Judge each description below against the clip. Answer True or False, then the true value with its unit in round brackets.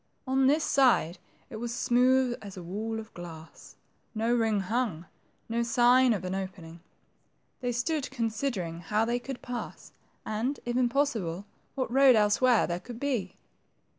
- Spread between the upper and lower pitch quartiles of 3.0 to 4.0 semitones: False (4.7 semitones)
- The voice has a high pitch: True (230 Hz)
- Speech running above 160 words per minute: False (150 wpm)